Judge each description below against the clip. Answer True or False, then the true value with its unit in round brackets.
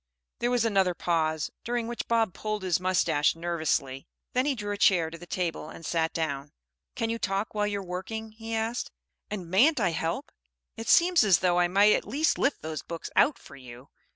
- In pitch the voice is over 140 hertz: True (190 Hz)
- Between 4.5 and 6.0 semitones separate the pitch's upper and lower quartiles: True (5.4 semitones)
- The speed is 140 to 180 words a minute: False (205 wpm)